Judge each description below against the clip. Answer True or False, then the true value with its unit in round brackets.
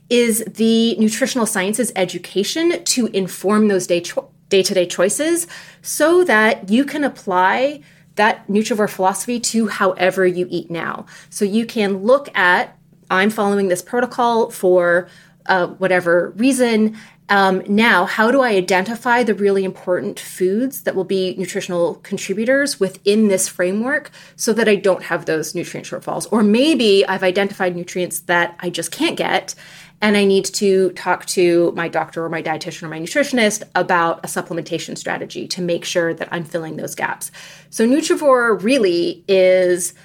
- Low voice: False (190 Hz)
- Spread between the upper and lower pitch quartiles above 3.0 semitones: True (3.9 semitones)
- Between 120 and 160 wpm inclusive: True (155 wpm)